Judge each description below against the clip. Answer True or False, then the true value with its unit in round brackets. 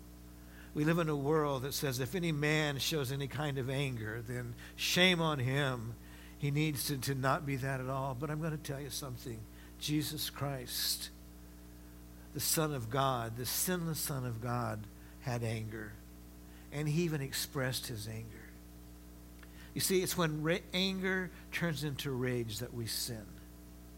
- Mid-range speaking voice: False (130 Hz)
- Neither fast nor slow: True (165 wpm)